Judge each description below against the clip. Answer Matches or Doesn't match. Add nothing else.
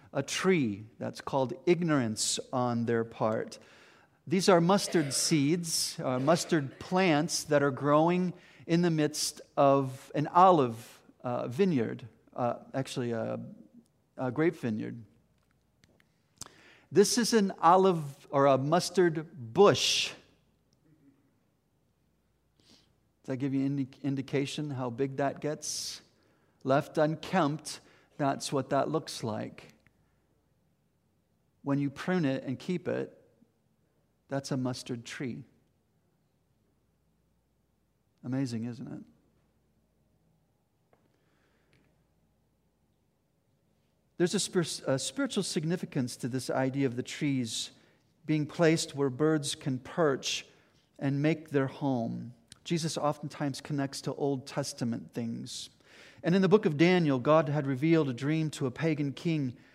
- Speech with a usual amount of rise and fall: Matches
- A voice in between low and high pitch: Matches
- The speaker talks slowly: Matches